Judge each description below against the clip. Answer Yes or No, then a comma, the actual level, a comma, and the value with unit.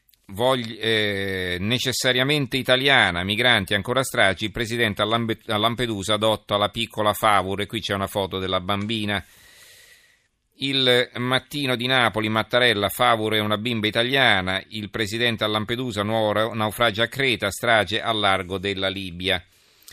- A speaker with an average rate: Yes, average, 130 wpm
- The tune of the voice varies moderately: Yes, average, 3.3 semitones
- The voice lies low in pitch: Yes, low, 110 Hz